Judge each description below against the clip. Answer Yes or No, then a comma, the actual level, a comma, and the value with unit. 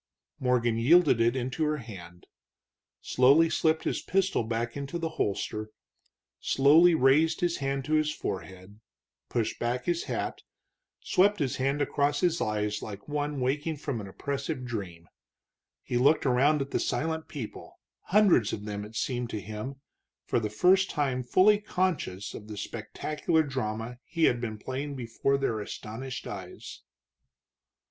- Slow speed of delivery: No, average, 150 wpm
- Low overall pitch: Yes, low, 130 Hz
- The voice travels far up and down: Yes, wide, 5.7 semitones